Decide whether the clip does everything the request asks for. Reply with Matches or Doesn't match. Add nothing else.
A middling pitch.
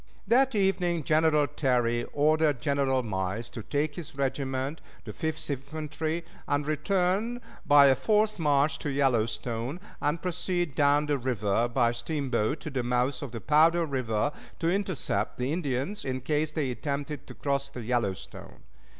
Matches